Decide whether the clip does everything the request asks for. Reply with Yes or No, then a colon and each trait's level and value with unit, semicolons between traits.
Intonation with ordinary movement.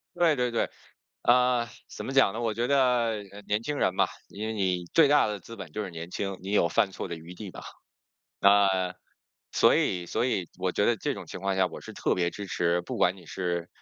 Yes: average, 4.5 semitones